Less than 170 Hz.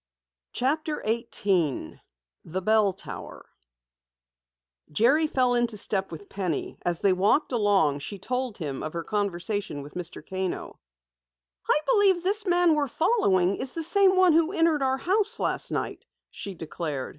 No: high, 215 Hz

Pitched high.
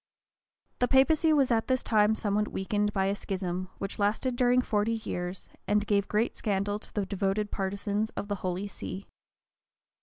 Yes: high, 205 Hz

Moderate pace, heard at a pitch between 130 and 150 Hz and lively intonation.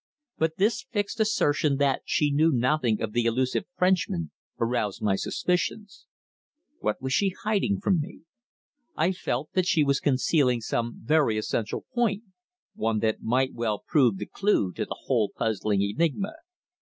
Yes: average, 155 wpm; medium, 140 Hz; wide, 7.9 semitones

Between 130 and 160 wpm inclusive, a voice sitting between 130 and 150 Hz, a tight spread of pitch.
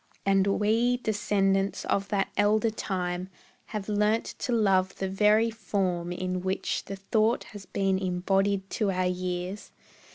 No: average, 140 wpm; high, 195 Hz; narrow, 2.1 semitones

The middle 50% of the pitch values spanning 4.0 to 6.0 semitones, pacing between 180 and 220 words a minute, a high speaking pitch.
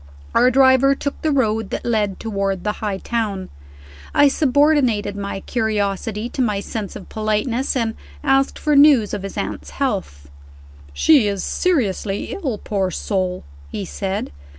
No: average, 5.1 semitones; average, 150 wpm; high, 215 Hz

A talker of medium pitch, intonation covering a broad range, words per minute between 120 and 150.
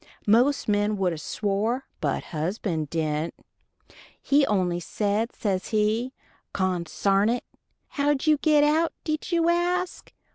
No: high, 215 Hz; wide, 7.6 semitones; slow, 135 wpm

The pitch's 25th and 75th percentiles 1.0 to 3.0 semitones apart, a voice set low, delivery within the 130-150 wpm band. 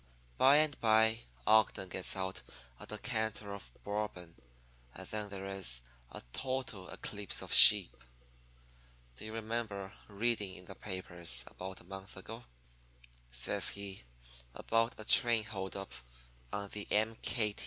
Yes: narrow, 2.6 semitones; low, 100 Hz; slow, 135 wpm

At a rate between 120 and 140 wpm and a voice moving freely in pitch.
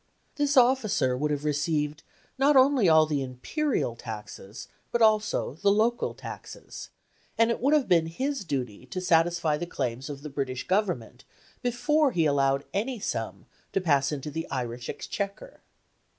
No: average, 155 wpm; wide, 9.0 semitones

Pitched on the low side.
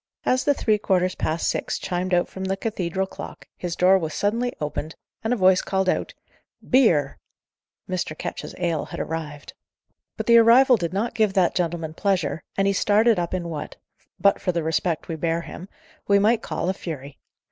No: medium, 185 Hz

